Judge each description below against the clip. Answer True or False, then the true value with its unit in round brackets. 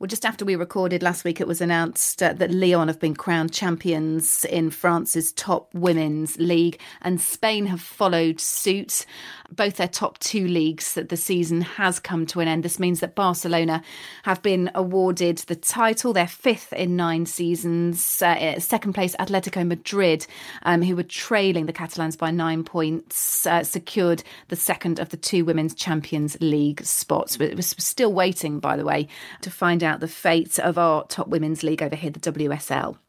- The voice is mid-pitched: True (170 Hz)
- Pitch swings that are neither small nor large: False (2.0 semitones)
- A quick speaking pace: False (180 wpm)